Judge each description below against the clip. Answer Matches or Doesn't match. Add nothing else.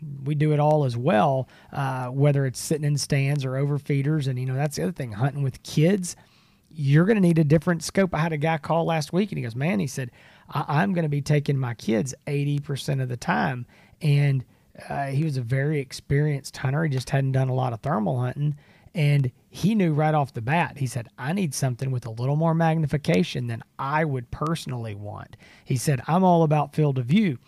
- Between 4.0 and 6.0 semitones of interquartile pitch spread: Doesn't match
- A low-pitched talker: Doesn't match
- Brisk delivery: Matches